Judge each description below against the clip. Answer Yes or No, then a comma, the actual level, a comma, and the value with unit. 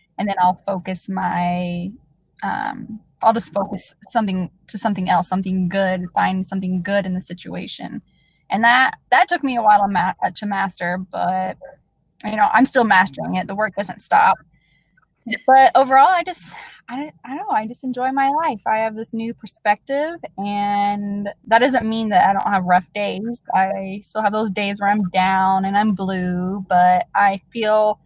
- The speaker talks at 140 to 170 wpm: No, average, 180 wpm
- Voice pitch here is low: No, high, 205 Hz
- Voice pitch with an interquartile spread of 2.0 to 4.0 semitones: Yes, average, 3.6 semitones